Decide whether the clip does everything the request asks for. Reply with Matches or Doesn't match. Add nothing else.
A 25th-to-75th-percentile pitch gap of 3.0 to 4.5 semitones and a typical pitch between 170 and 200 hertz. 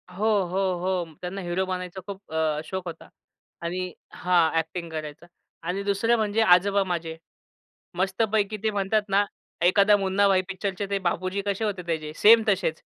Doesn't match